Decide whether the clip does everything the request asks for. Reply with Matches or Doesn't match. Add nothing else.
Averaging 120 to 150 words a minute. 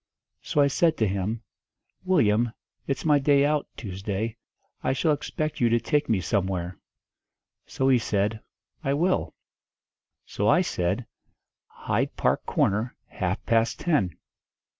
Matches